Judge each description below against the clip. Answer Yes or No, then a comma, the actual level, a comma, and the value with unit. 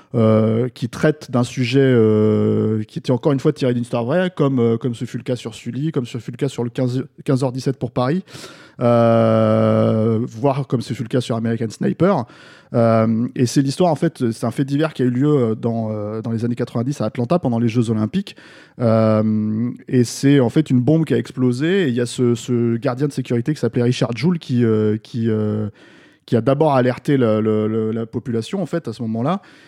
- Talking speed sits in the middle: No, fast, 225 wpm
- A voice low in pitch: Yes, low, 120 Hz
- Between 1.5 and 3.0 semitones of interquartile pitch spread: No, average, 3.4 semitones